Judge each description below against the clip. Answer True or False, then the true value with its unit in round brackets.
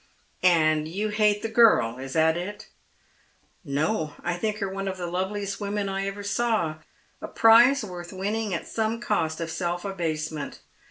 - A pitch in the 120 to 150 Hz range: False (195 Hz)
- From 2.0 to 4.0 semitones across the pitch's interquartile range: False (4.4 semitones)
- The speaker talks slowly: False (180 wpm)